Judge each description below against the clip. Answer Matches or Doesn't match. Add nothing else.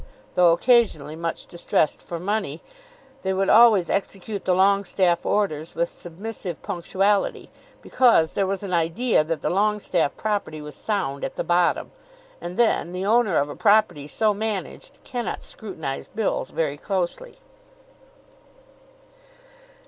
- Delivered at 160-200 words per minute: Doesn't match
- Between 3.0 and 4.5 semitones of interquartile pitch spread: Matches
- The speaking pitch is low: Doesn't match